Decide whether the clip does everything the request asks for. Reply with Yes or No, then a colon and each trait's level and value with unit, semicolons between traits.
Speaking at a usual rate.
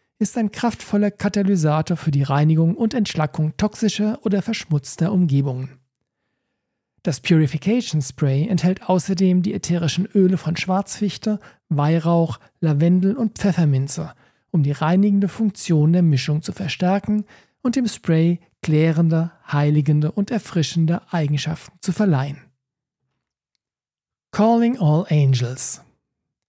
No: slow, 110 wpm